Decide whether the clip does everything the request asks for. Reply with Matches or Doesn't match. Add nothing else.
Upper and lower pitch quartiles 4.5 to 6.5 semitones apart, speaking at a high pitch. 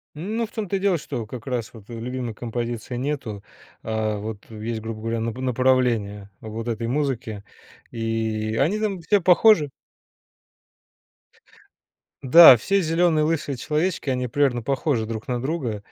Doesn't match